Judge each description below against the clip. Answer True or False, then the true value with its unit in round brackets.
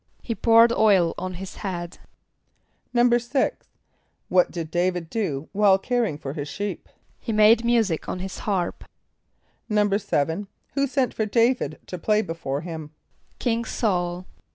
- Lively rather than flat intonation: False (4.7 semitones)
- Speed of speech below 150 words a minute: True (135 wpm)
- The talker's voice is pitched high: True (200 Hz)